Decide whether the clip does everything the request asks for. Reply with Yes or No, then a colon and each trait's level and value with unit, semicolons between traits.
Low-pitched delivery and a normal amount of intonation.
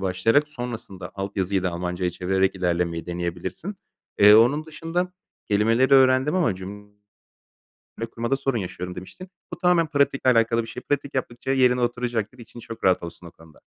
No: low, 115 Hz; wide, 6.1 semitones